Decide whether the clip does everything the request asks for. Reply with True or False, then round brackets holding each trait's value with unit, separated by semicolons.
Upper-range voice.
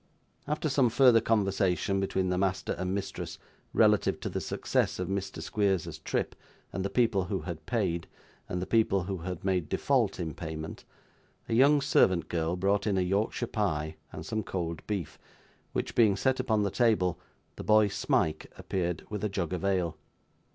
False (95 Hz)